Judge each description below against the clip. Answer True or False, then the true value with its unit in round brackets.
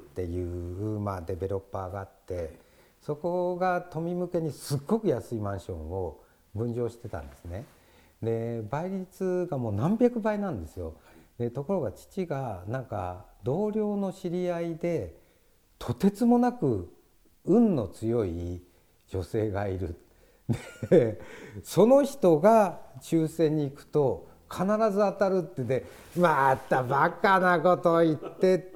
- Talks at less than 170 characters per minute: False (230 characters per minute)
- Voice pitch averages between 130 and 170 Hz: True (140 Hz)